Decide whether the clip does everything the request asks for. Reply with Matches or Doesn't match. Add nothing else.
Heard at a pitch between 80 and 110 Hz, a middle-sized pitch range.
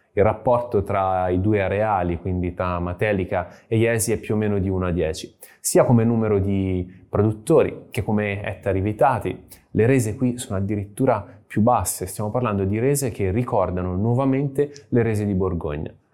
Matches